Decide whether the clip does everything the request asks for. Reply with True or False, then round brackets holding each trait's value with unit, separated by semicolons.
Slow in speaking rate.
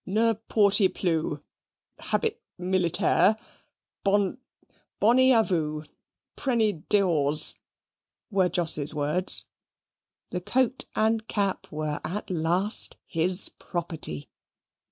True (90 wpm)